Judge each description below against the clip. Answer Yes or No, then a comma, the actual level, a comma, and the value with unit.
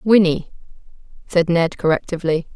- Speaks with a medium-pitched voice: Yes, medium, 170 Hz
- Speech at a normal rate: No, slow, 95 wpm